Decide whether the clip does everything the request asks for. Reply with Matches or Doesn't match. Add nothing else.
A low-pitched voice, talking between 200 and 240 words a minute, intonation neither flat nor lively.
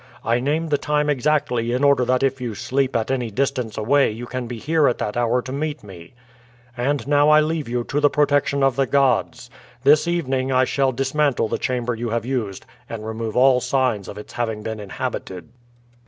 Matches